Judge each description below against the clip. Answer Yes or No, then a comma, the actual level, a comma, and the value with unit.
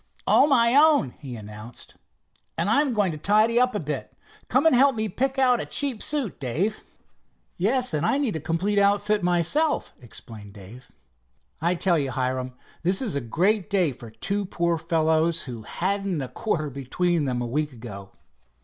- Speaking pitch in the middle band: Yes, medium, 175 Hz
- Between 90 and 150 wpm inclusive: No, average, 175 wpm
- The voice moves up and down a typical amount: No, wide, 8.2 semitones